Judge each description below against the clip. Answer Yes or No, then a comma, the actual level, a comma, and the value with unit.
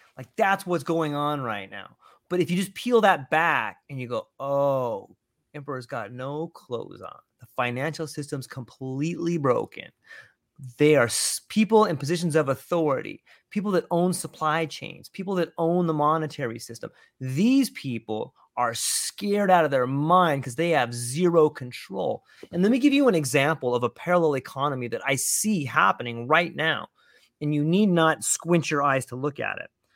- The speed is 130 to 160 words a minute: No, average, 175 wpm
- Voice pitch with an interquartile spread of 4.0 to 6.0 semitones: Yes, average, 4.7 semitones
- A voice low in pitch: No, medium, 155 Hz